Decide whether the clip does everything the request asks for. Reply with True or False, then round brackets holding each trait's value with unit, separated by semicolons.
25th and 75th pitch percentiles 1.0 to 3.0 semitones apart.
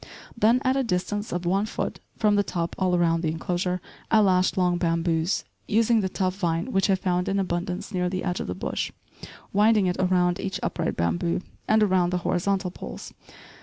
True (2.5 semitones)